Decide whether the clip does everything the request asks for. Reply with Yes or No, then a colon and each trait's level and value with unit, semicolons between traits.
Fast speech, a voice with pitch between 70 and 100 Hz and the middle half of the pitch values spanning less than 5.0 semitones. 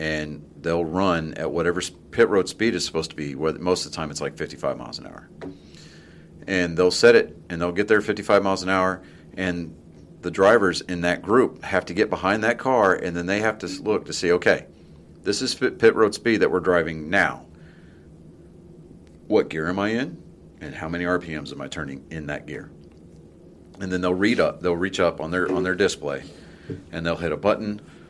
Yes: fast, 210 wpm; very low, 90 Hz; narrow, 2.6 semitones